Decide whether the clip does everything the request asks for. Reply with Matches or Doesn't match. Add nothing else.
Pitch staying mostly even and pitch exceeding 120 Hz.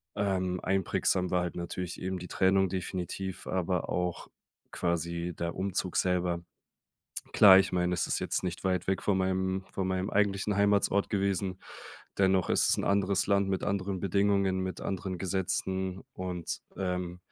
Doesn't match